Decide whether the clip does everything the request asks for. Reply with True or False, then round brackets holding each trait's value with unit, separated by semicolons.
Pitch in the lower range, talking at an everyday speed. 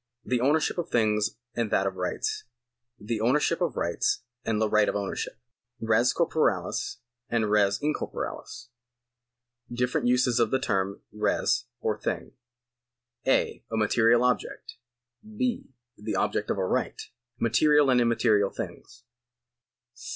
False (115 Hz; 130 wpm)